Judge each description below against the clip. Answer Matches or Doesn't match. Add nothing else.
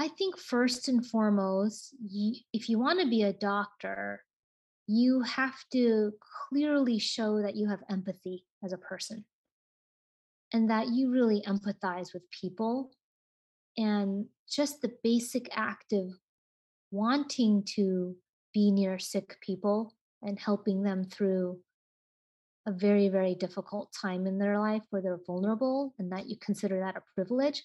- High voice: Matches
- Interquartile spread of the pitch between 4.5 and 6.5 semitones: Doesn't match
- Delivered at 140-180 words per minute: Matches